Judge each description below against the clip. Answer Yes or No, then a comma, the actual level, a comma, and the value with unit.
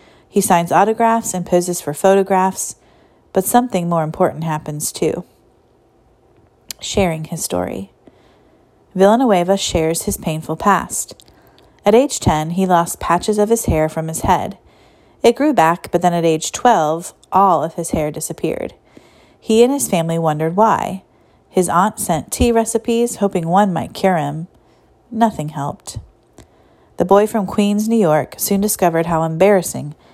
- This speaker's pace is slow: No, average, 145 wpm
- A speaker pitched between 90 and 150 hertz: No, medium, 180 Hz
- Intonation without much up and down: No, average, 4.4 semitones